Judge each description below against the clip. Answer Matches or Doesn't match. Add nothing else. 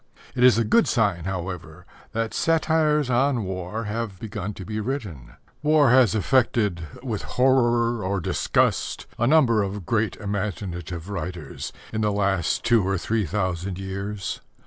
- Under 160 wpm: Matches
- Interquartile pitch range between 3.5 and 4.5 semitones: Matches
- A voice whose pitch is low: Matches